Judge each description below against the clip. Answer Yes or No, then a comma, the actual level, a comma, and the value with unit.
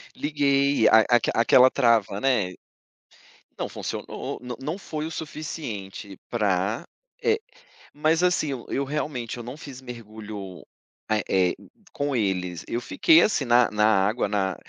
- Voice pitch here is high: No, low, 120 Hz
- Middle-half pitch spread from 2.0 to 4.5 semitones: No, wide, 5.4 semitones